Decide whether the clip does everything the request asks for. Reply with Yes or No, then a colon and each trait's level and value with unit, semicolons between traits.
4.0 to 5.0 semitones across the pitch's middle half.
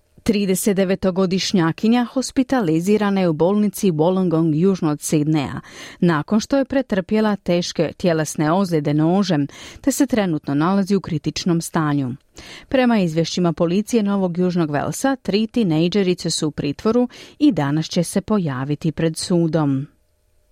Yes: average, 4.7 semitones